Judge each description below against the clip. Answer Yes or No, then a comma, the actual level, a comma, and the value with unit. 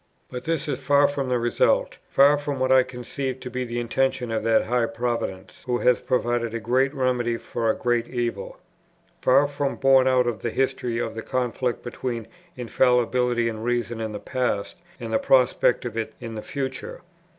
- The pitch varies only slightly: Yes, narrow, 2.0 semitones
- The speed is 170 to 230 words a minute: Yes, average, 190 wpm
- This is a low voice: Yes, low, 125 Hz